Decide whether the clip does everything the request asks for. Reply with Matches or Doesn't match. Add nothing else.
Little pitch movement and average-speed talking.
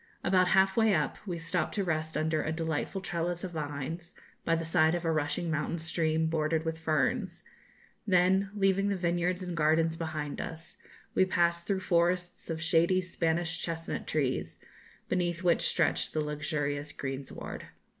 Matches